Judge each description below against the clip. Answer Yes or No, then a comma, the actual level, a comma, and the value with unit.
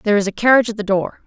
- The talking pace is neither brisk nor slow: No, fast, 330 wpm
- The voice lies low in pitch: No, high, 215 Hz